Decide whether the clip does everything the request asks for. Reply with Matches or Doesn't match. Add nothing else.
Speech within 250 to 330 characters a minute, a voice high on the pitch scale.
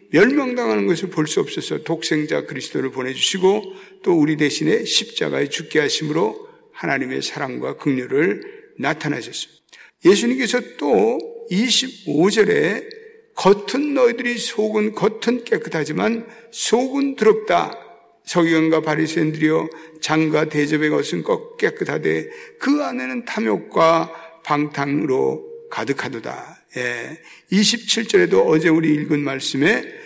Matches